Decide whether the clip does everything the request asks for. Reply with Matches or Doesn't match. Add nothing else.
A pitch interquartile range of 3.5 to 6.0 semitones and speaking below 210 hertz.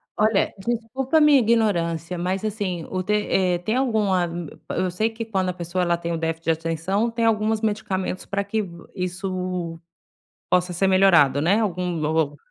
Matches